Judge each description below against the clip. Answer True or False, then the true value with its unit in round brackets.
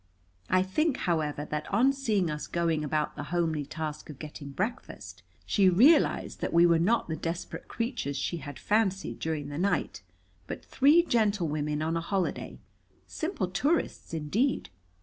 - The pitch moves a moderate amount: False (6.2 semitones)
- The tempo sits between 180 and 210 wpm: False (155 wpm)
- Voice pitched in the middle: True (170 Hz)